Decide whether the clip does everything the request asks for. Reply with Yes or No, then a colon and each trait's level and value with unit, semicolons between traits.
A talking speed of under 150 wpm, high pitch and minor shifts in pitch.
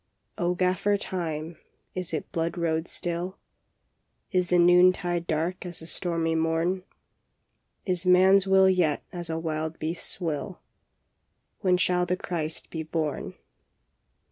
No: average, 140 wpm; medium, 175 Hz; narrow, 2.0 semitones